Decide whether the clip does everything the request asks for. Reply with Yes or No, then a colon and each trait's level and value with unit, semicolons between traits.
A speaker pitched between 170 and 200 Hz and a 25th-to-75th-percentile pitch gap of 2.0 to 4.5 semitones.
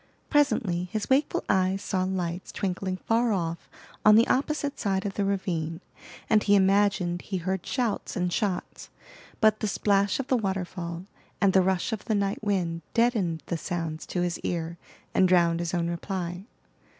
Yes: high, 190 Hz; average, 2.9 semitones